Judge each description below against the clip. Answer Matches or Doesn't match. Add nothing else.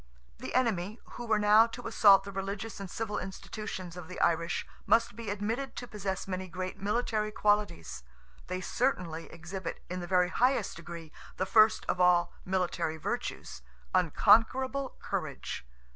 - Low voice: Doesn't match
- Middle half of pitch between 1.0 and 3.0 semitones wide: Doesn't match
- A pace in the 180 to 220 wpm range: Doesn't match